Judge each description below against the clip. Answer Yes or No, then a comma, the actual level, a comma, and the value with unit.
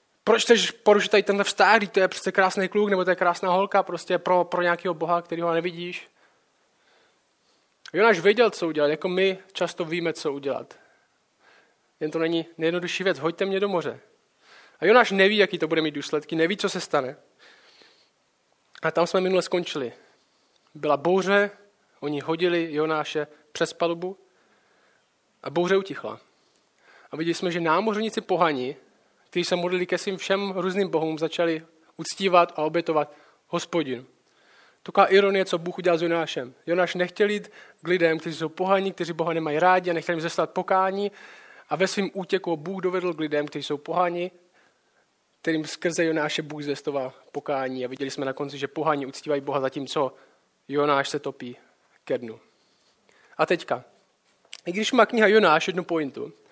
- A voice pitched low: No, medium, 175 Hz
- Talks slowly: No, average, 165 wpm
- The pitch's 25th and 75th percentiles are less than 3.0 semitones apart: No, average, 3.3 semitones